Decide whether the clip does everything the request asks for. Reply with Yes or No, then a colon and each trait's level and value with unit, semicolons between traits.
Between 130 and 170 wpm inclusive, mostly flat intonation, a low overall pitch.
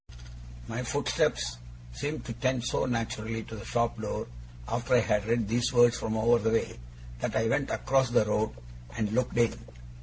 No: average, 180 wpm; narrow, 1.7 semitones; low, 115 Hz